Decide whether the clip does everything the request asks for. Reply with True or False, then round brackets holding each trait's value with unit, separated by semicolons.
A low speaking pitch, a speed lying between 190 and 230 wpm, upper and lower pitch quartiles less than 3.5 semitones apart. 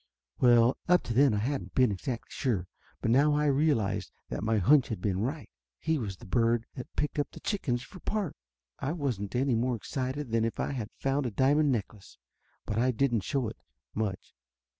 False (125 Hz; 195 wpm; 4.2 semitones)